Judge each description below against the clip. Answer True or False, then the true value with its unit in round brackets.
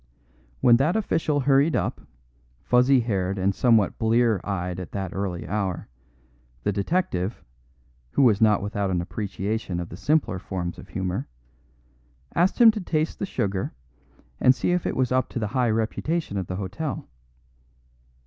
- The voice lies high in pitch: False (110 Hz)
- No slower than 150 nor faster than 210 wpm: True (160 wpm)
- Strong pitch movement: True (6.0 semitones)